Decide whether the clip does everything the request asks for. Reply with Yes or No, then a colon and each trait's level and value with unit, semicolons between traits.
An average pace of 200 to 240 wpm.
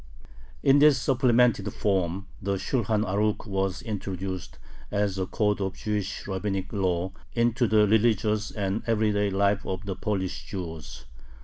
No: slow, 135 wpm